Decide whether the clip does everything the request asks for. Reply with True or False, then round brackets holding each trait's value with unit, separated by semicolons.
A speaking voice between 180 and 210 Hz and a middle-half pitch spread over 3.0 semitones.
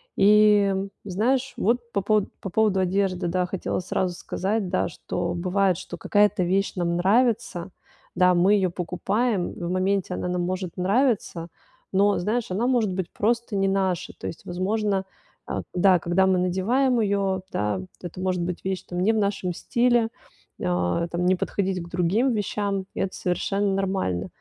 False (190 Hz; 2.6 semitones)